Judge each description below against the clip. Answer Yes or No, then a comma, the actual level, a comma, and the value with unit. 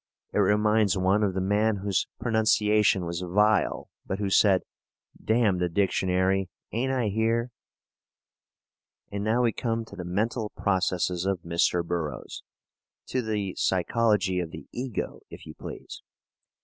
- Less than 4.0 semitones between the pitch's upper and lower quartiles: Yes, average, 3.2 semitones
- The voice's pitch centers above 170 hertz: No, low, 100 Hz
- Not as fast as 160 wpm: Yes, average, 140 wpm